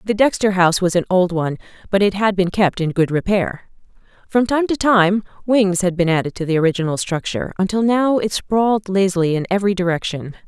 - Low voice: No, high, 190 Hz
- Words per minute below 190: No, average, 200 wpm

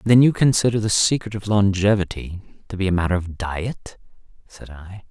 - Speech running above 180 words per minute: No, average, 175 wpm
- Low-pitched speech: Yes, low, 100 Hz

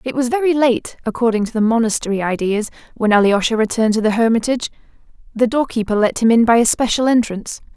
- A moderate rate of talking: Yes, average, 195 wpm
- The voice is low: No, high, 230 Hz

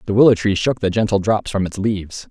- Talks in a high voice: No, low, 100 Hz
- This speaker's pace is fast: Yes, fast, 260 wpm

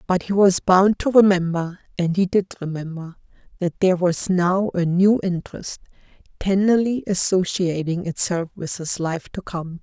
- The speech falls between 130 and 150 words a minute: Yes, average, 140 wpm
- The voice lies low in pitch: No, medium, 180 Hz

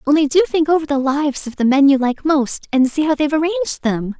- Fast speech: Yes, fast, 255 wpm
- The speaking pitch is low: No, very high, 290 Hz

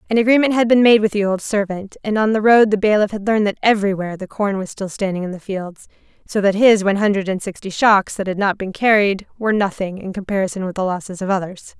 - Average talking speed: No, fast, 250 wpm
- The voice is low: No, high, 200 Hz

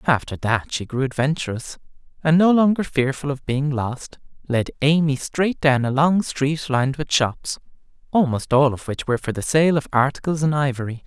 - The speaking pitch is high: No, medium, 140 Hz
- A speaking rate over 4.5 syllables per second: Yes, 5.1 syllables/s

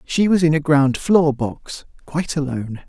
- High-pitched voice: No, medium, 150 Hz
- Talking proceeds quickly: No, average, 190 wpm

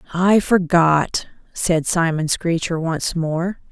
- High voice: No, medium, 170 Hz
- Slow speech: Yes, slow, 115 wpm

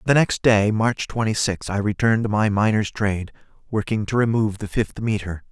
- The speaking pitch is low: Yes, low, 105 Hz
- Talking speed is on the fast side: No, average, 195 wpm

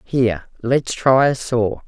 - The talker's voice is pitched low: Yes, low, 120 Hz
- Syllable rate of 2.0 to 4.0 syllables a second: Yes, 3.7 syllables/s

